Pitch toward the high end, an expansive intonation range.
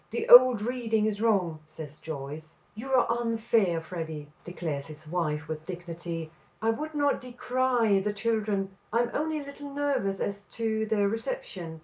Yes: high, 210 Hz; wide, 6.4 semitones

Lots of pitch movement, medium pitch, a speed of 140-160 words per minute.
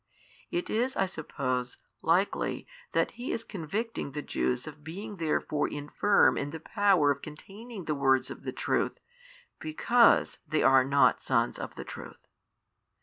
Yes: wide, 6.1 semitones; medium, 160 Hz; average, 150 wpm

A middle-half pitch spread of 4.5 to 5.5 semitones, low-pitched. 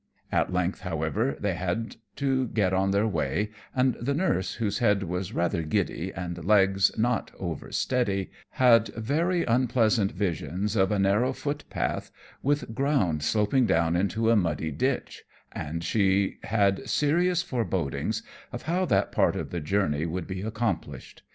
Yes: average, 5.1 semitones; low, 100 Hz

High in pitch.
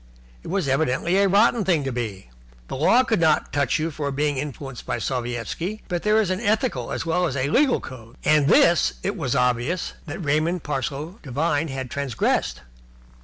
No: medium, 150 Hz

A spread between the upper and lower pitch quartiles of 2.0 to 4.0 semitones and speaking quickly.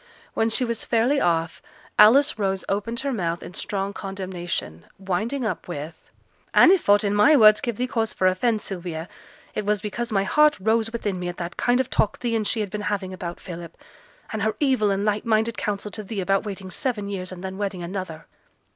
Yes: average, 3.4 semitones; fast, 210 wpm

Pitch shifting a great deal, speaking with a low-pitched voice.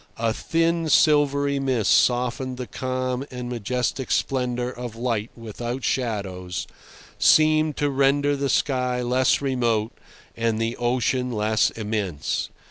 No: average, 2.9 semitones; low, 125 Hz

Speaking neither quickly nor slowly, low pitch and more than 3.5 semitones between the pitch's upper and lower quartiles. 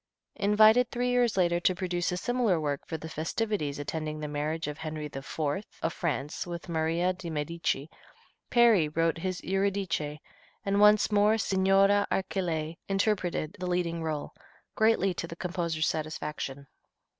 No: average, 145 wpm; medium, 175 Hz; average, 4.0 semitones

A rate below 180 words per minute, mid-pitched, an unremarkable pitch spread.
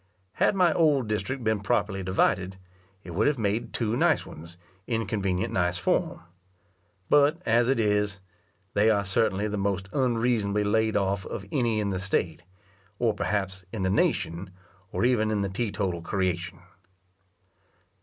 No: average, 155 wpm; low, 105 Hz; average, 3.1 semitones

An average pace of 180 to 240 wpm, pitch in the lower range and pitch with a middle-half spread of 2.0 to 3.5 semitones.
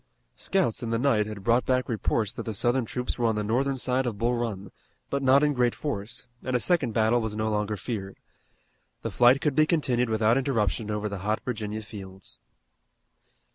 Yes: average, 200 wpm; low, 115 Hz; average, 3.2 semitones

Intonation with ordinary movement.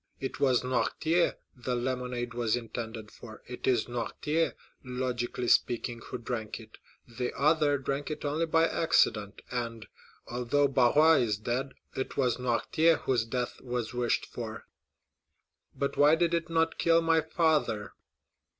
Yes: average, 4.0 semitones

